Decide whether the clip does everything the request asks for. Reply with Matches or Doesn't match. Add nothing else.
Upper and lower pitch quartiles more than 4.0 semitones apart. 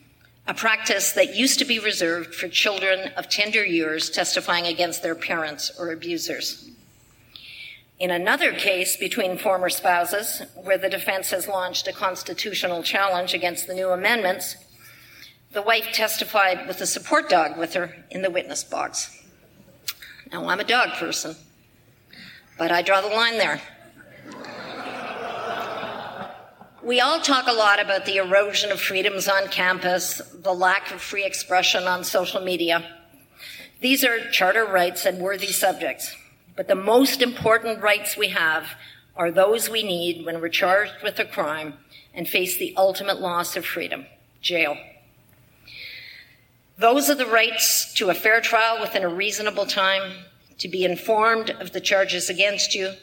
Doesn't match